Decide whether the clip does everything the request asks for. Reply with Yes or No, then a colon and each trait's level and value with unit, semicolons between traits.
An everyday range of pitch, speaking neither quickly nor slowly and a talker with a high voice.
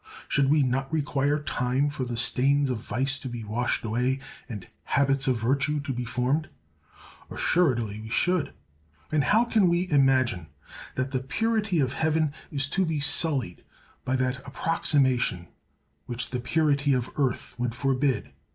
No: average, 3.1 semitones; average, 155 wpm; low, 135 Hz